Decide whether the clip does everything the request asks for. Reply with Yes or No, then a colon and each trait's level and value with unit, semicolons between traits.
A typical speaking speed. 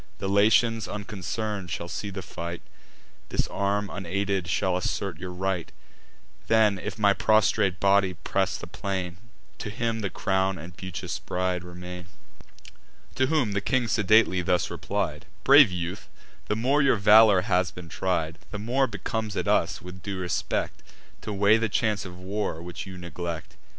Yes: average, 160 wpm